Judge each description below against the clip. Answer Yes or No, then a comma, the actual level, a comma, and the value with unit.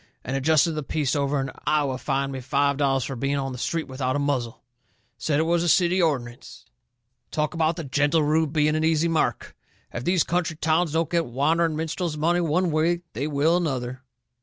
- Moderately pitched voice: Yes, medium, 150 Hz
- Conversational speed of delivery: No, fast, 210 wpm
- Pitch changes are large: No, average, 3.1 semitones